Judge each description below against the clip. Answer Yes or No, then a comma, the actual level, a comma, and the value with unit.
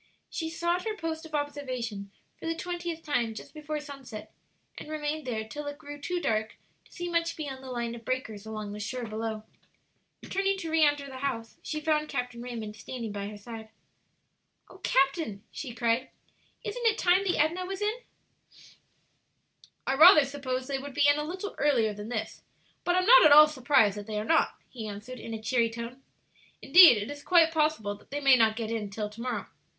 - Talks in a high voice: Yes, very high, 270 Hz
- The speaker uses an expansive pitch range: Yes, wide, 5.8 semitones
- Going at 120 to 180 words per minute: No, average, 200 wpm